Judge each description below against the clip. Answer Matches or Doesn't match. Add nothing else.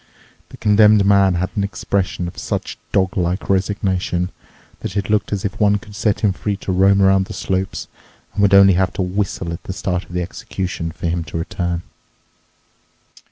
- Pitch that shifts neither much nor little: Doesn't match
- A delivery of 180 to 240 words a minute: Matches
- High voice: Doesn't match